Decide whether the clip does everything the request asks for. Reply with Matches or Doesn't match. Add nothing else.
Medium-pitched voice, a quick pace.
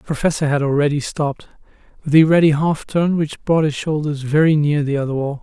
Matches